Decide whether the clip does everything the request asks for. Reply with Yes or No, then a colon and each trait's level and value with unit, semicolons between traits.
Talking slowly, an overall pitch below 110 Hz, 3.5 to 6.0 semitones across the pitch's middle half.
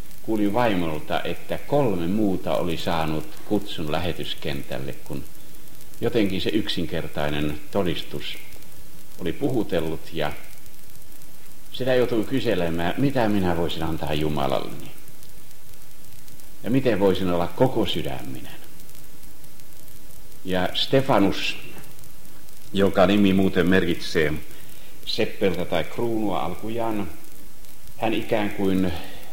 Yes: slow, 90 wpm; very low, 90 Hz; average, 5.2 semitones